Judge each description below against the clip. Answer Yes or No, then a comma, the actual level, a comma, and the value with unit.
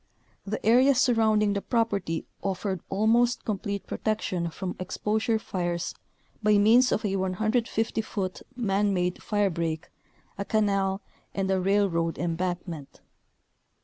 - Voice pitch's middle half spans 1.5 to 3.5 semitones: Yes, average, 2.9 semitones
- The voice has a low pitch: No, high, 200 Hz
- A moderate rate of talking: No, slow, 120 wpm